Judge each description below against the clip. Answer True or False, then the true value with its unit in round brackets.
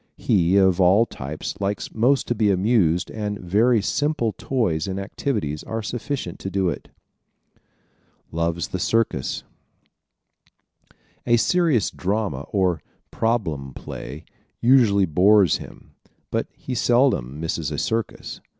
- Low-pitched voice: True (100 Hz)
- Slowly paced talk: True (125 wpm)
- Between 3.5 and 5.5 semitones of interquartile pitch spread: True (5.2 semitones)